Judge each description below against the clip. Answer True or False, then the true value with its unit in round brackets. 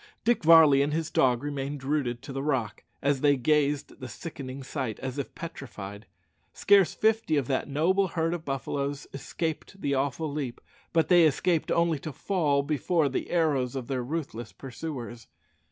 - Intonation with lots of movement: False (3.5 semitones)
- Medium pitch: True (145 Hz)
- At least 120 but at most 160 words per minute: False (170 wpm)